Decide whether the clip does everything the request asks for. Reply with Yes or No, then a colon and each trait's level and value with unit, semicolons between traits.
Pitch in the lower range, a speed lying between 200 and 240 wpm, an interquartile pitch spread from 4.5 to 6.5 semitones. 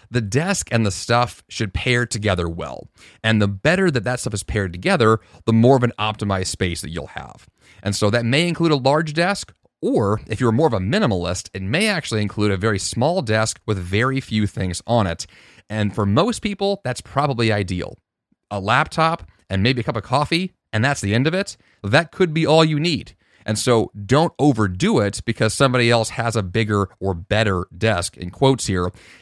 Yes: low, 110 Hz; fast, 205 wpm; average, 5.1 semitones